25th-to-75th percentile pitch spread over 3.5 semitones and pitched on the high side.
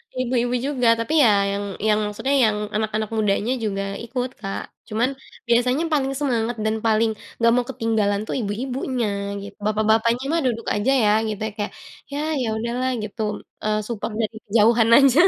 No: average, 2.7 semitones; high, 230 Hz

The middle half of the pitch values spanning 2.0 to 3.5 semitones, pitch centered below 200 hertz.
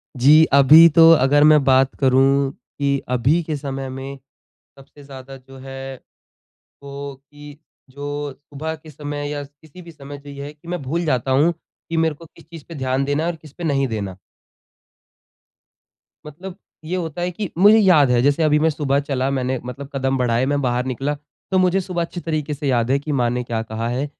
Yes: average, 2.8 semitones; medium, 140 Hz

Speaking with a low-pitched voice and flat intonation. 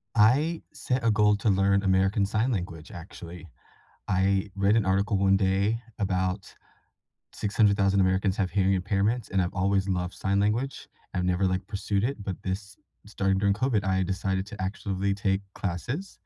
Yes: low, 100 Hz; narrow, 1.7 semitones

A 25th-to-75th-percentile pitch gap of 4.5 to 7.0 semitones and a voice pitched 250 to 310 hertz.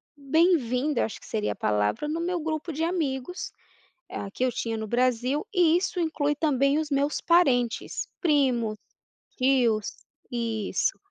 Yes: average, 5.1 semitones; very high, 275 Hz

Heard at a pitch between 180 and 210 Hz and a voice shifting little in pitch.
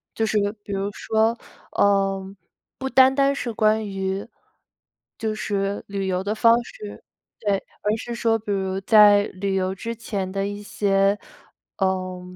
Yes: high, 205 Hz; narrow, 2.2 semitones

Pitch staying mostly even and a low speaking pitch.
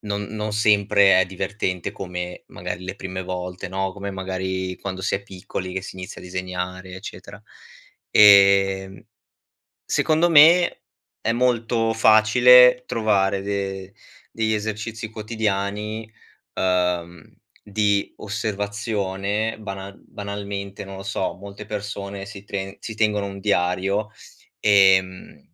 Yes: narrow, 2.2 semitones; low, 100 Hz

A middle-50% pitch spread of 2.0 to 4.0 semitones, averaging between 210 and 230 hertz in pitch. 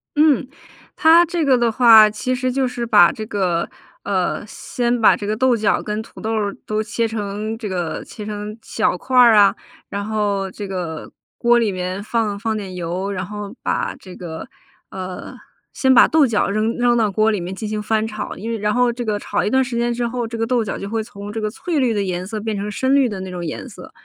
Yes: average, 3.0 semitones; high, 215 Hz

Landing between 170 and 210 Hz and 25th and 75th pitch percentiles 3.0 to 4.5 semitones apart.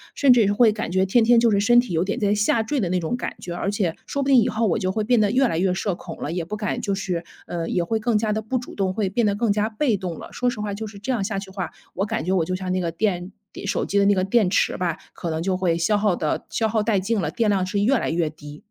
Yes: high, 200 Hz; average, 3.3 semitones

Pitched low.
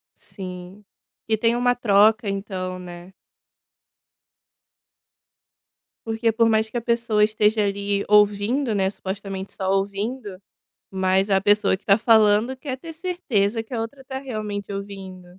No: high, 210 Hz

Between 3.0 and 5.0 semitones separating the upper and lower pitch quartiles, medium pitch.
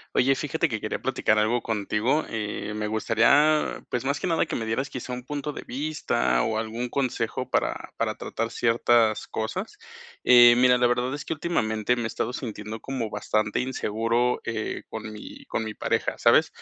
No: average, 3.3 semitones; low, 120 Hz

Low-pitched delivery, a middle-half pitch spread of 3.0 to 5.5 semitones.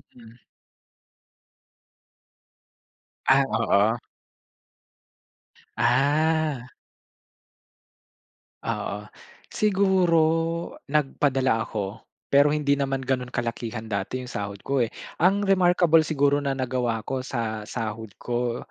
Yes: low, 130 Hz; average, 4.4 semitones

